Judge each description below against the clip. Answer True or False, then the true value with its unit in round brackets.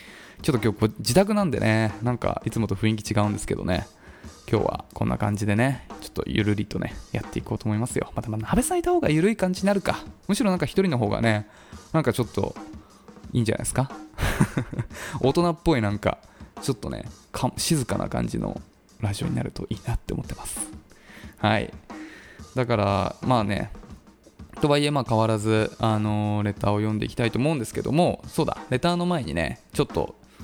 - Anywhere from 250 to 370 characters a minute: False (390 characters per minute)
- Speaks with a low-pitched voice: True (110 Hz)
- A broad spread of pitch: True (6.0 semitones)